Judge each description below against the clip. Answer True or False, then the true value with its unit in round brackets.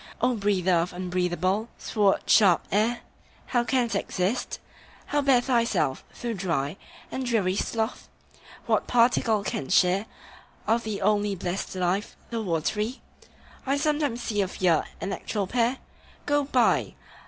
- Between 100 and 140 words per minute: True (135 wpm)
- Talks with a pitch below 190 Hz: False (210 Hz)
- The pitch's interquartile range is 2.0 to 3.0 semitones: False (4.4 semitones)